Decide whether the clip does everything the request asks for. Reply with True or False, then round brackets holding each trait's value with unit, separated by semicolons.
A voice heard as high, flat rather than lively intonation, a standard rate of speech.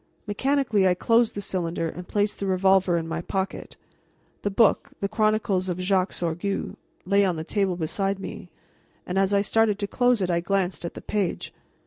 True (195 Hz; 2.3 semitones; 185 wpm)